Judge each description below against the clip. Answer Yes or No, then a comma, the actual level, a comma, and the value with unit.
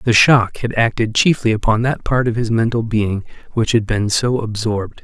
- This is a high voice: No, low, 115 Hz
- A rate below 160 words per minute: No, fast, 205 wpm